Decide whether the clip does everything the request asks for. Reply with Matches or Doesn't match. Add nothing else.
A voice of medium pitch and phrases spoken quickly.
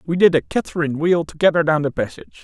Matches